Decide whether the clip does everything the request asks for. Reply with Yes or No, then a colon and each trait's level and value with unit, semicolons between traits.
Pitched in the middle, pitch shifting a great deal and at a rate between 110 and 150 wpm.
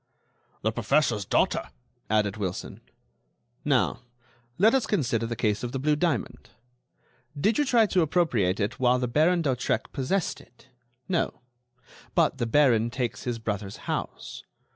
No: low, 125 Hz; wide, 6.1 semitones; average, 140 wpm